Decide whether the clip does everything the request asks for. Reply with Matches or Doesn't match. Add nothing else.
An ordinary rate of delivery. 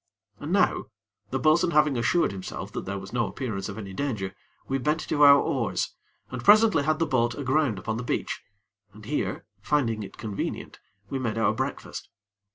Matches